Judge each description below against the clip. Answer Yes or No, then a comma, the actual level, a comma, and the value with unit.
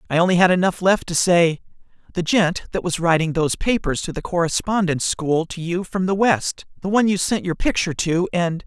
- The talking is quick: Yes, fast, 215 wpm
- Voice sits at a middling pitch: Yes, medium, 180 Hz